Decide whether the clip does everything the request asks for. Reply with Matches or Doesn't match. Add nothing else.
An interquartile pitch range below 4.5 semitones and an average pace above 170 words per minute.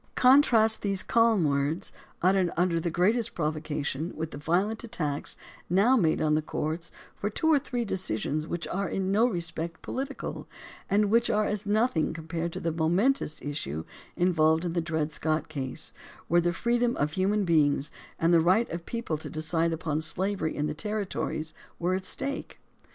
Doesn't match